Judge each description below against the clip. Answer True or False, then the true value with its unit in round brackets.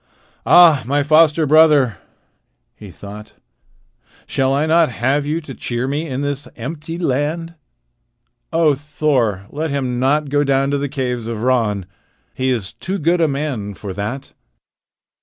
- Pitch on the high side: False (140 Hz)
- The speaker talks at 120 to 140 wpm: False (150 wpm)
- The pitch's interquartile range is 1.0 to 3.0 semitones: False (3.6 semitones)